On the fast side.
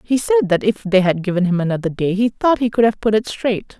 Yes: fast, 285 wpm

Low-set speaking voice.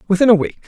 No: medium, 185 Hz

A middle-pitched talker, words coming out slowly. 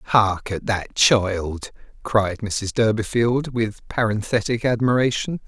No: low, 110 Hz; slow, 110 wpm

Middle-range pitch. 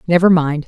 Yes: medium, 165 Hz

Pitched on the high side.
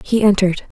Yes: high, 200 Hz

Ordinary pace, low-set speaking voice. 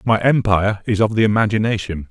Yes: average, 170 wpm; low, 105 Hz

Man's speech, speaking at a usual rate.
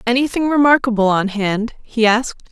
No: female; average, 145 wpm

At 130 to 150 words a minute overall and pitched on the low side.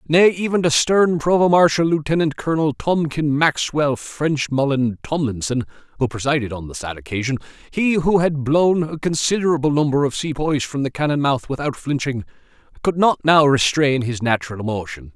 No: average, 145 wpm; medium, 145 Hz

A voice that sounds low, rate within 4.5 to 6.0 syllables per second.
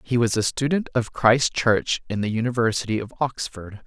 Yes: low, 120 Hz; 5.0 syllables/s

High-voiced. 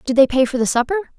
Yes: very high, 275 Hz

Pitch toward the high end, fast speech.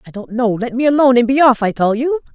Yes: very high, 250 Hz; fast, 305 wpm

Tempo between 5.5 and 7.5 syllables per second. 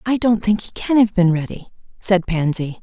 No: 5.2 syllables/s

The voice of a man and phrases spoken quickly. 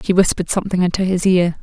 No: female; fast, 220 wpm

